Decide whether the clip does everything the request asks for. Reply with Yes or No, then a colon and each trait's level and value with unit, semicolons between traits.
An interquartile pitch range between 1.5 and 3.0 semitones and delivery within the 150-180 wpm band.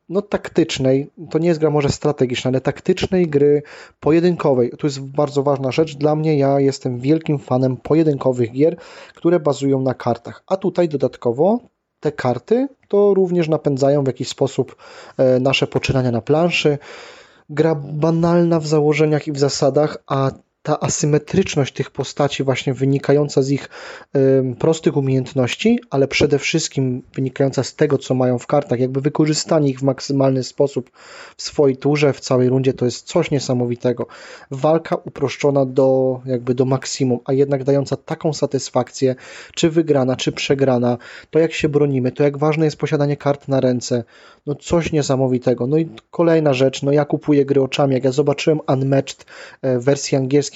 Yes: average, 2.7 semitones; fast, 160 wpm